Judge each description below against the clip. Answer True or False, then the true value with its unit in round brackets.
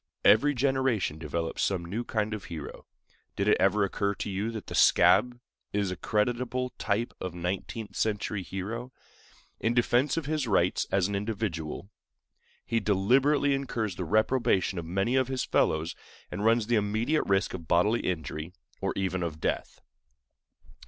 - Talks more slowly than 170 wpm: True (160 wpm)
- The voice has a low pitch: True (105 Hz)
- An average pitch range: True (4.5 semitones)